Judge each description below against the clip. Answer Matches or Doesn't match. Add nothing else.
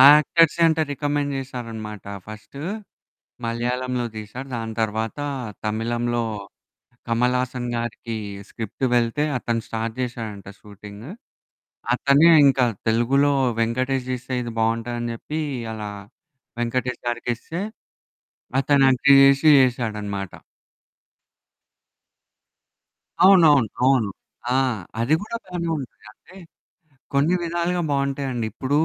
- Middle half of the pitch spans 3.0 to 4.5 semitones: Matches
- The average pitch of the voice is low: Matches